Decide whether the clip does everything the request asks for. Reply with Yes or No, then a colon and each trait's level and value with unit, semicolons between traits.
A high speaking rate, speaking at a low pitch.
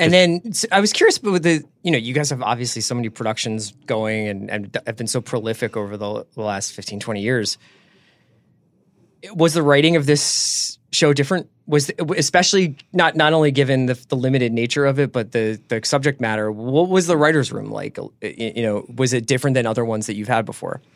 Yes: fast, 215 wpm; low, 130 Hz